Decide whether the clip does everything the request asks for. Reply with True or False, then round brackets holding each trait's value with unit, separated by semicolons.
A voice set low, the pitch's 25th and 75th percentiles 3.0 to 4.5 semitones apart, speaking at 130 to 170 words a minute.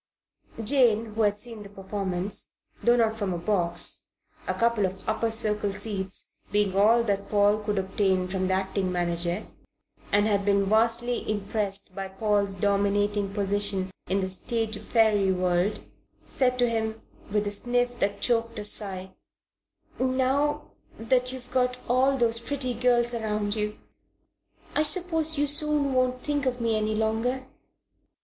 False (215 Hz; 3.5 semitones; 150 wpm)